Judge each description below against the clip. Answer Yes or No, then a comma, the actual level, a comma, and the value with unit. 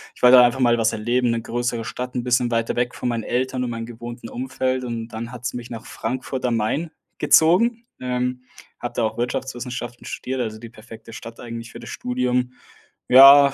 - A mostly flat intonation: Yes, narrow, 1.4 semitones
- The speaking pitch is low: Yes, low, 120 Hz